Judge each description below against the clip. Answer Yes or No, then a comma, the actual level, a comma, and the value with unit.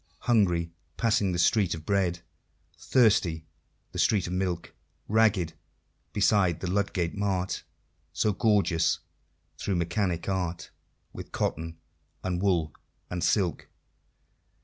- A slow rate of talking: Yes, slow, 110 wpm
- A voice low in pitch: Yes, very low, 90 Hz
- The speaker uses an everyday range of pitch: Yes, average, 3.0 semitones